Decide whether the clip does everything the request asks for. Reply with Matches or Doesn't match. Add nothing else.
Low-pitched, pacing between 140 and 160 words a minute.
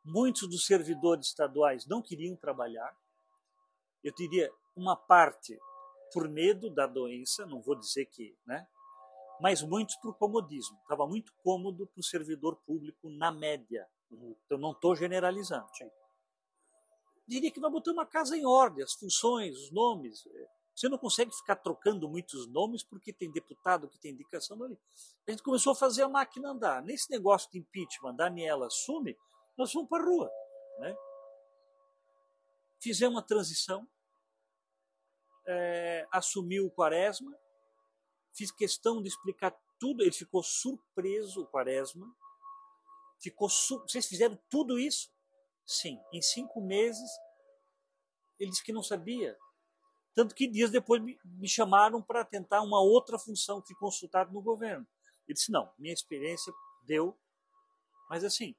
Doesn't match